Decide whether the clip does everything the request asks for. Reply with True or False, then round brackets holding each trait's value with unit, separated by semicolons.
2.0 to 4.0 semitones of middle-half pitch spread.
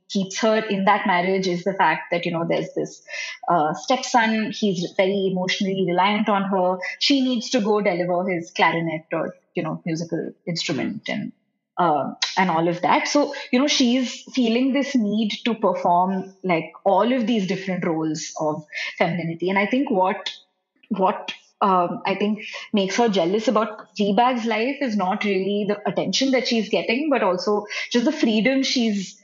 False (4.7 semitones)